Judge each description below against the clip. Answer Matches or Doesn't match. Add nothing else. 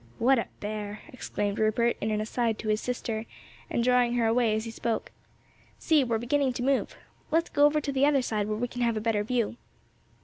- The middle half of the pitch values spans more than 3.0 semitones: Doesn't match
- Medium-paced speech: Doesn't match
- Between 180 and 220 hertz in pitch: Doesn't match